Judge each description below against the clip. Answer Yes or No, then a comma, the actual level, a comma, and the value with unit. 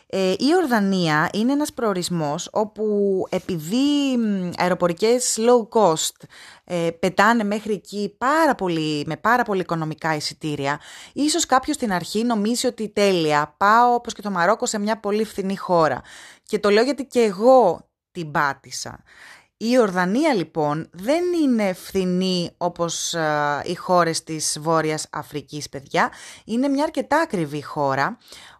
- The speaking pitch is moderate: No, high, 195 Hz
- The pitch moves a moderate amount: No, wide, 6.4 semitones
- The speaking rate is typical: Yes, average, 140 wpm